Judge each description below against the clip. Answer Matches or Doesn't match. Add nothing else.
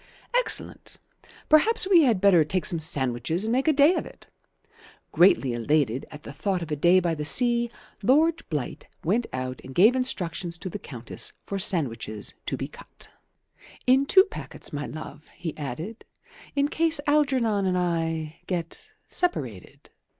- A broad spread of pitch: Matches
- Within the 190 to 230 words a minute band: Doesn't match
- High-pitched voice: Doesn't match